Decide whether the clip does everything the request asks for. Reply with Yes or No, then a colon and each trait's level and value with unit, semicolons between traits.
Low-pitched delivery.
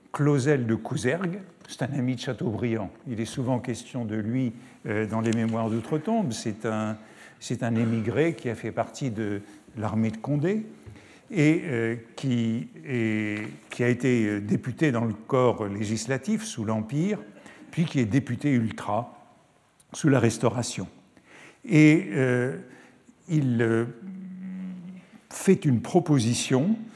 Yes: low, 125 Hz